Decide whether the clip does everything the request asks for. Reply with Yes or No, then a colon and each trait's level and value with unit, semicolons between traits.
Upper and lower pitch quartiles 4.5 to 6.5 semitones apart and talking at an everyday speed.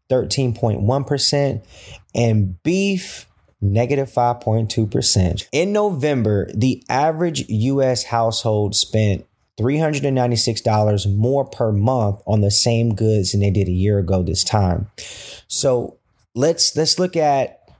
No: average, 4.8 semitones; slow, 110 wpm